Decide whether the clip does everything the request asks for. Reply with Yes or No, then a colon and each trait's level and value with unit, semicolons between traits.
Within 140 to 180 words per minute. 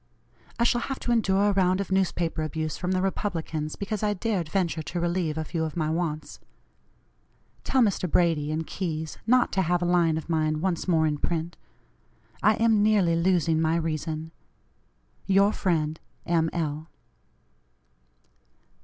Yes: average, 160 wpm